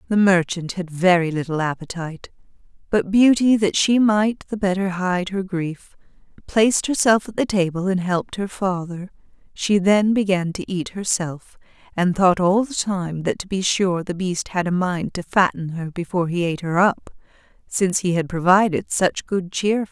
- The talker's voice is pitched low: No, medium, 185 Hz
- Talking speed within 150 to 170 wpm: No, average, 185 wpm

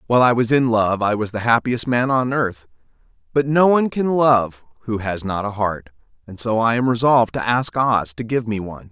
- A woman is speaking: No, male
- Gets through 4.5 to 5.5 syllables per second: Yes, 5.3 syllables/s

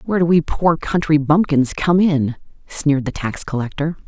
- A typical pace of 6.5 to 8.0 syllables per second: No, 5.0 syllables/s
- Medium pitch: Yes, medium, 155 Hz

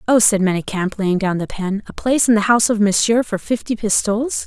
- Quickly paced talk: Yes, fast, 230 wpm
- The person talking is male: No, female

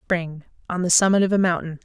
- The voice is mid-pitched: Yes, medium, 175 Hz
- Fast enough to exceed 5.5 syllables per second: Yes, 5.9 syllables/s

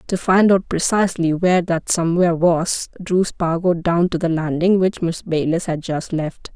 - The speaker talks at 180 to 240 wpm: Yes, average, 185 wpm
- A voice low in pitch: No, medium, 170 Hz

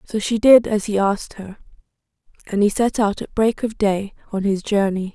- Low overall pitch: No, high, 205 Hz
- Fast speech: Yes, fast, 210 wpm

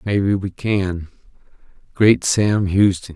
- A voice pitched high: No, low, 100 Hz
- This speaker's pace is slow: Yes, slow, 95 wpm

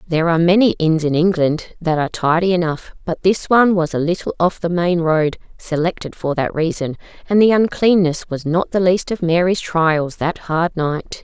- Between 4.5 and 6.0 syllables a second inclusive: Yes, 5.0 syllables/s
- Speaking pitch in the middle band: Yes, medium, 170 Hz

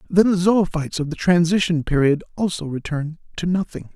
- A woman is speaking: No, male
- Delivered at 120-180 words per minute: Yes, average, 165 wpm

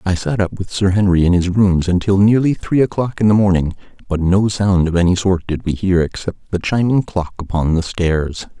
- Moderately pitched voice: No, very low, 95 Hz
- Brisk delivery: Yes, fast, 225 wpm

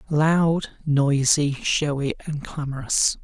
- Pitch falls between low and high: Yes, medium, 145 Hz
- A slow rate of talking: Yes, slow, 95 wpm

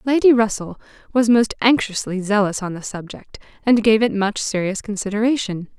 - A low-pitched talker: No, high, 215 Hz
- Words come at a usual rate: Yes, average, 155 wpm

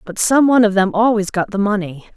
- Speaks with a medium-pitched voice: No, high, 205 Hz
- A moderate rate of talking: No, fast, 250 wpm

